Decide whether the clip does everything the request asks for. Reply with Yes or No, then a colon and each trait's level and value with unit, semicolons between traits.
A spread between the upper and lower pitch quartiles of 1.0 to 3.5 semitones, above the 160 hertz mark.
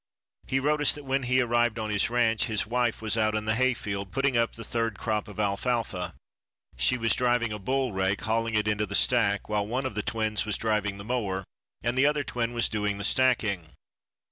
No: average, 2.9 semitones; low, 115 Hz